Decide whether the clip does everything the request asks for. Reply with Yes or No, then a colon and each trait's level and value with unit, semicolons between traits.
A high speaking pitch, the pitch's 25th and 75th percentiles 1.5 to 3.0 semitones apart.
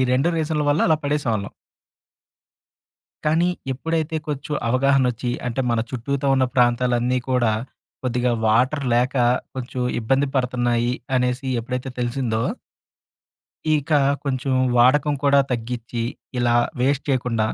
No: low, 125 Hz; narrow, 2.5 semitones